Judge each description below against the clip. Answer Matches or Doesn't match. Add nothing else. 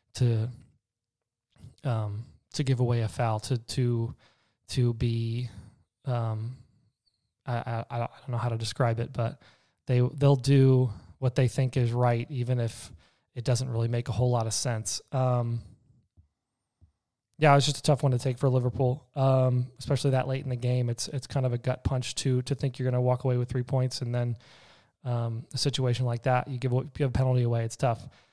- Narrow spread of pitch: Matches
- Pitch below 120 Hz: Doesn't match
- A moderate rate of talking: Matches